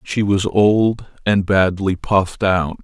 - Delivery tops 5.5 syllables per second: No, 3.5 syllables/s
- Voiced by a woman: No, male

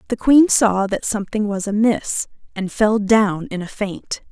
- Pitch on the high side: Yes, high, 210 Hz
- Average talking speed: Yes, average, 180 wpm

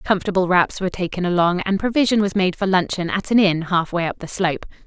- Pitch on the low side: No, medium, 185 Hz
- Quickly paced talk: Yes, fast, 235 wpm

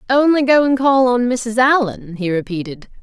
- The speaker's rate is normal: Yes, average, 180 wpm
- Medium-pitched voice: No, high, 240 Hz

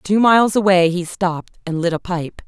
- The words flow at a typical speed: No, fast, 220 wpm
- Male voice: No, female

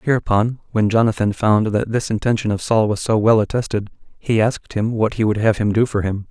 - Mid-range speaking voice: No, low, 110 Hz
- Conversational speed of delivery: No, fast, 230 wpm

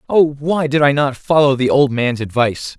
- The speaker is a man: Yes, male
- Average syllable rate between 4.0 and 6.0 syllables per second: Yes, 5.0 syllables/s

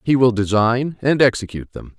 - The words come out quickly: No, average, 180 wpm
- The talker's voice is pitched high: No, low, 120 Hz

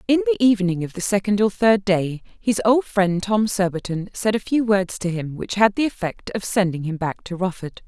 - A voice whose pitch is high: Yes, high, 200 Hz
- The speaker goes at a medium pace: No, fast, 230 wpm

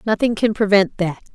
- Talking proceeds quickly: No, average, 180 wpm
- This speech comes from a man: No, female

